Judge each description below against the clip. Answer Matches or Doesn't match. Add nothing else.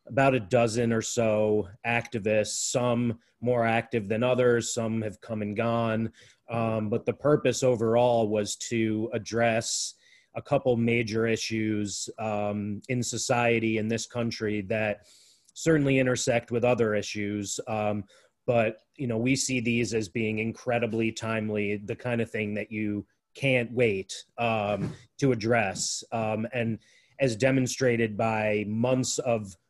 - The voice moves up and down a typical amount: Doesn't match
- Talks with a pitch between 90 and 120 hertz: Matches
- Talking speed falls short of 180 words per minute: Matches